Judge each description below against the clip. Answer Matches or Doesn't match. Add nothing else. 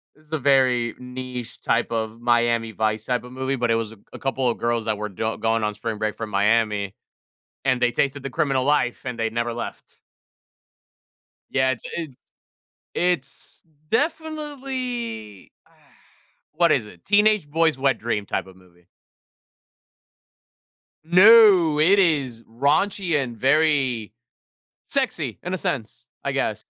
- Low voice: Matches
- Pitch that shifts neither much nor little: Doesn't match